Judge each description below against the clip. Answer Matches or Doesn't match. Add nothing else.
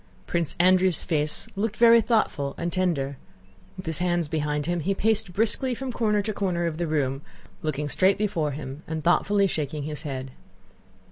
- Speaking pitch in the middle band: Matches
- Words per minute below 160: Doesn't match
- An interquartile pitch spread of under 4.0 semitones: Doesn't match